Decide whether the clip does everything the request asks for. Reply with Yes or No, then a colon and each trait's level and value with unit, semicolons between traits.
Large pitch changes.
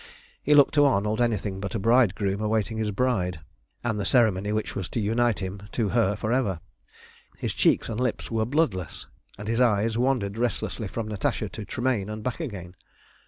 No: average, 3.3 semitones